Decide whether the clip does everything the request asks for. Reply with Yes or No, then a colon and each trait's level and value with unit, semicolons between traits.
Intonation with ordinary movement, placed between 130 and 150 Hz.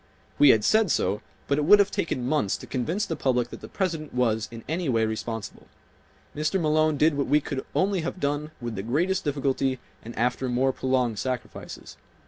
Yes: average, 4.3 semitones; medium, 140 Hz